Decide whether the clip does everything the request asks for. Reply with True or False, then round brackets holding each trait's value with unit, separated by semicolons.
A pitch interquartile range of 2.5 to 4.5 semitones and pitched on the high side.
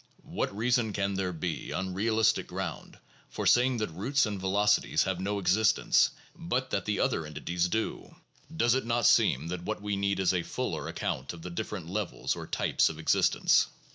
False (3.5 semitones; 100 Hz)